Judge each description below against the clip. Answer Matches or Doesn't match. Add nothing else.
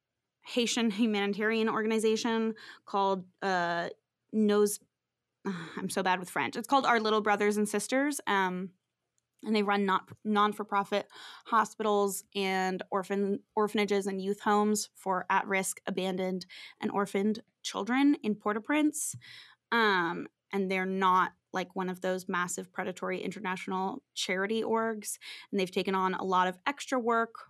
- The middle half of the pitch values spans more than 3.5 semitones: Doesn't match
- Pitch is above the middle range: Matches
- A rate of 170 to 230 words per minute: Doesn't match